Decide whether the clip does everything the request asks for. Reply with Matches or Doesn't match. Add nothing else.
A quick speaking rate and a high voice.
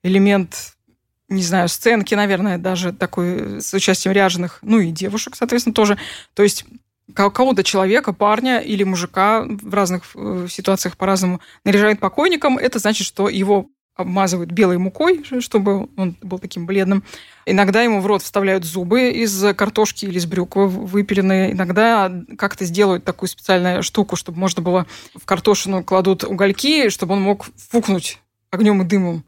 Doesn't match